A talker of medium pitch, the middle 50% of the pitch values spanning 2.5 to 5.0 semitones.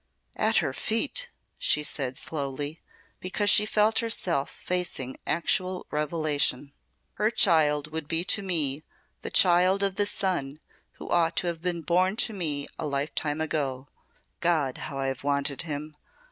Yes: medium, 160 Hz; average, 4.4 semitones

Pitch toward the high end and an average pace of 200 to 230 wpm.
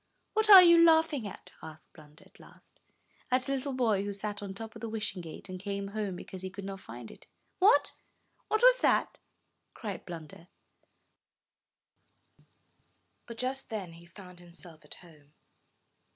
No: high, 200 Hz; average, 165 wpm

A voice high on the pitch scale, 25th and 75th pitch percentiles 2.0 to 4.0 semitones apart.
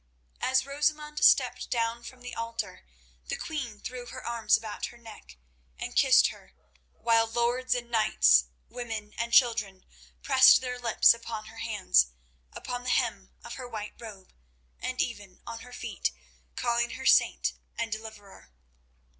Yes: high, 230 Hz; narrow, 2.5 semitones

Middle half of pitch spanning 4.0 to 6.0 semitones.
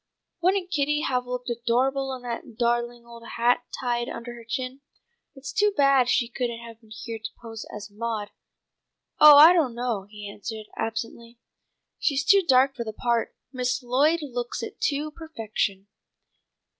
No: average, 3.0 semitones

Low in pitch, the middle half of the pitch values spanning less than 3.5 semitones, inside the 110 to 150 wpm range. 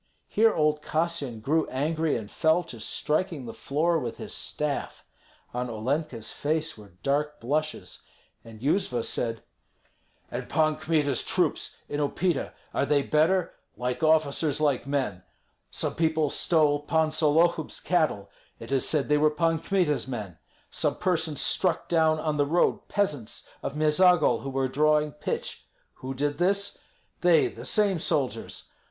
No: medium, 150 Hz; average, 3.1 semitones; average, 145 wpm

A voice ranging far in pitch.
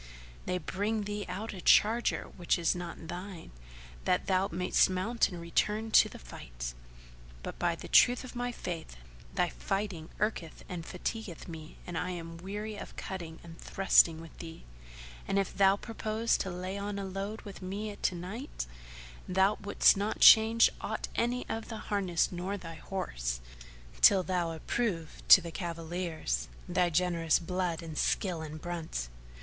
No: average, 3.5 semitones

